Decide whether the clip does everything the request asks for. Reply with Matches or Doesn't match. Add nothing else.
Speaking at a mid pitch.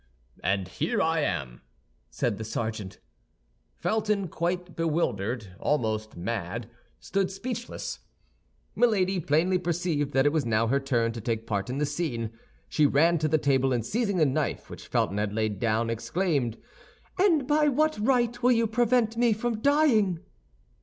Matches